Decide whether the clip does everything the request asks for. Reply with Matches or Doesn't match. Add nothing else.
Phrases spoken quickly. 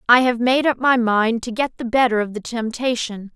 Matches